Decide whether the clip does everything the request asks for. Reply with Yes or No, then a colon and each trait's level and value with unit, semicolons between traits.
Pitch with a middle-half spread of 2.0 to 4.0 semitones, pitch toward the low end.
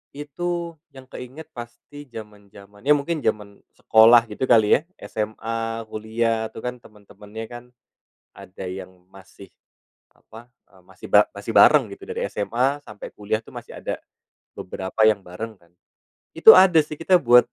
No: average, 4.7 semitones; low, 115 Hz